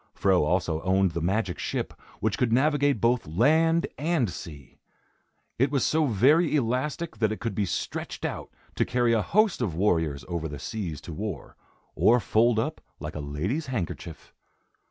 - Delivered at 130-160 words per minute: No, average, 170 wpm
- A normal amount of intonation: No, wide, 7.4 semitones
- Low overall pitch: Yes, low, 110 Hz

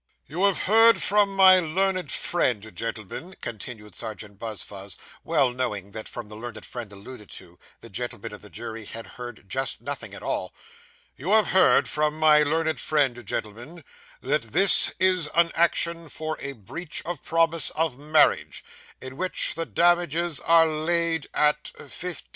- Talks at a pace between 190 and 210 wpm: No, average, 160 wpm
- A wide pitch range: Yes, wide, 6.7 semitones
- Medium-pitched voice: Yes, medium, 150 Hz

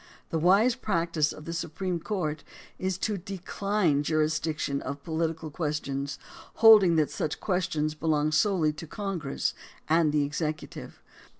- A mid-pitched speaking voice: Yes, medium, 160 Hz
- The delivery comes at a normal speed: No, slow, 130 wpm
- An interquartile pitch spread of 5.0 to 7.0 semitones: No, average, 3.4 semitones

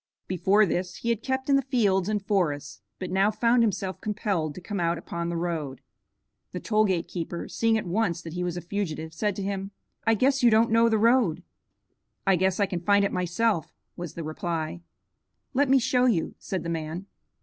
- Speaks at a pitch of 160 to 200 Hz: Yes, high, 190 Hz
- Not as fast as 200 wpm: No, fast, 205 wpm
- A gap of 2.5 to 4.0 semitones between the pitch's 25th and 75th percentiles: No, average, 4.5 semitones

